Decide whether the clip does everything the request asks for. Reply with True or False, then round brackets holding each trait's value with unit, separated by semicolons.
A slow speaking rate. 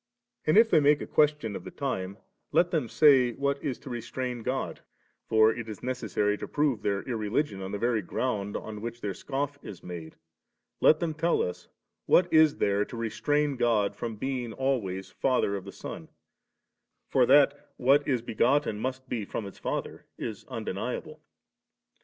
False (175 wpm)